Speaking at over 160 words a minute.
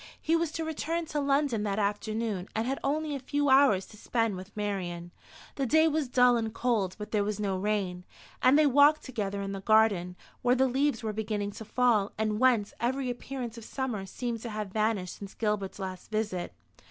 Yes: average, 200 wpm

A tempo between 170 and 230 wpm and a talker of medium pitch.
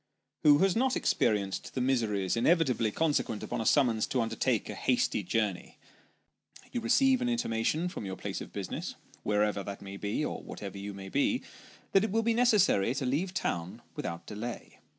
No: average, 175 wpm; low, 120 Hz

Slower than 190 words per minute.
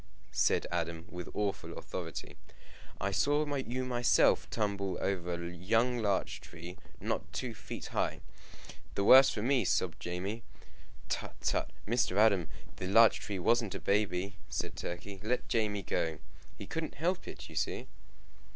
Yes: average, 150 wpm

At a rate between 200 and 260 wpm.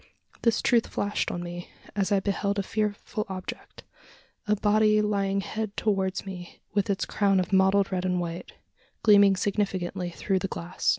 No: average, 165 wpm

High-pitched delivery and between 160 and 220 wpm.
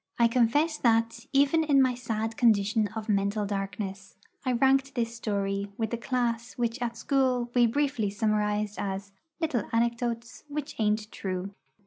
No: high, 230 Hz; average, 150 wpm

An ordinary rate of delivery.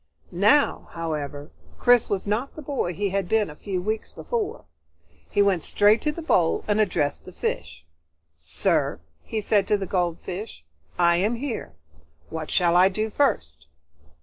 Yes: average, 160 wpm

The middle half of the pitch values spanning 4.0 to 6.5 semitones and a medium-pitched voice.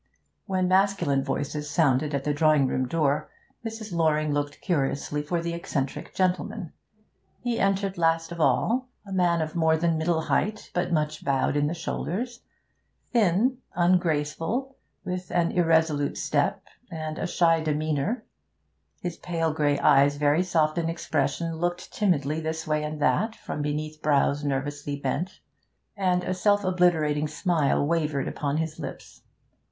No: average, 3.3 semitones; medium, 160 Hz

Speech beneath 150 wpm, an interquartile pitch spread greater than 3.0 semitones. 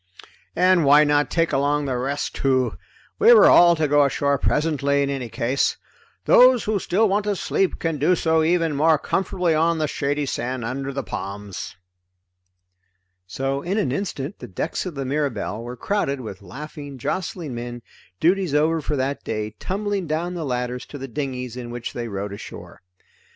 No: average, 175 wpm; average, 4.7 semitones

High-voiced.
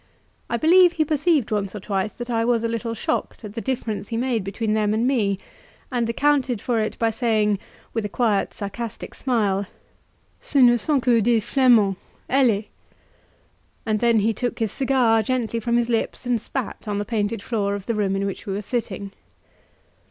Yes: high, 230 Hz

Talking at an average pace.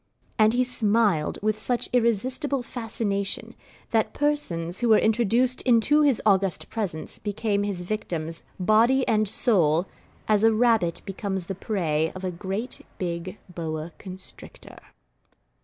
No: slow, 130 wpm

